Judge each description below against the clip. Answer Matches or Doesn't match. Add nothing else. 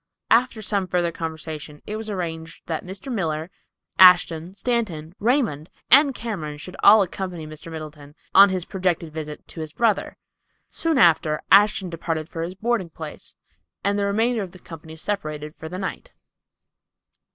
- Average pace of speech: Matches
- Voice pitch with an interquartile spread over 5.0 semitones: Doesn't match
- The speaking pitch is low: Doesn't match